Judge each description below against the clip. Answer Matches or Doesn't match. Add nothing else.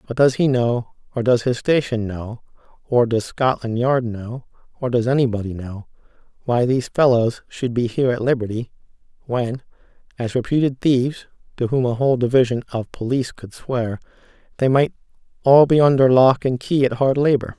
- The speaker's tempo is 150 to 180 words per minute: Matches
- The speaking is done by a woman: Doesn't match